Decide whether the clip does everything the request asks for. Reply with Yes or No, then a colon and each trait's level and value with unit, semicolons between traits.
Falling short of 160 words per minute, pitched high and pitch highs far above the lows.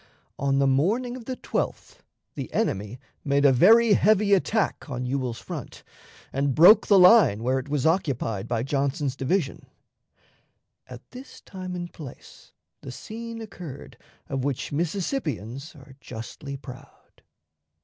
No: average, 140 wpm; medium, 140 Hz; wide, 6.7 semitones